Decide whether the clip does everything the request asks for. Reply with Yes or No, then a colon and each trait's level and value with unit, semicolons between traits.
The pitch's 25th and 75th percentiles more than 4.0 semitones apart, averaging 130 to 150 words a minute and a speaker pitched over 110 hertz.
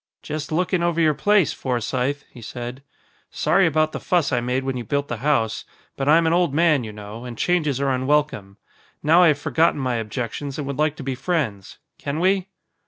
No: average, 4.4 semitones; fast, 205 wpm; medium, 140 Hz